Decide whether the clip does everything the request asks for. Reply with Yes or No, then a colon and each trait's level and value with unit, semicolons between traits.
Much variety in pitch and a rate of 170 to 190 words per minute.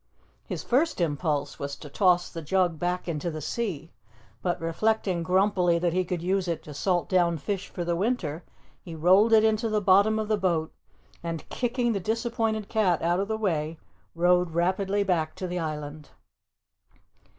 No: average, 3.7 semitones; average, 175 wpm